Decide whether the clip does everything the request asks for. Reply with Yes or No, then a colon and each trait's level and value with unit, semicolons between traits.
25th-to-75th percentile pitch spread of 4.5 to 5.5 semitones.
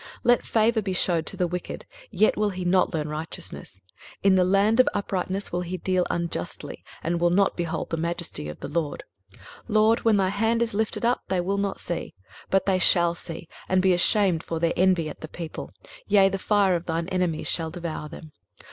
No: average, 3.0 semitones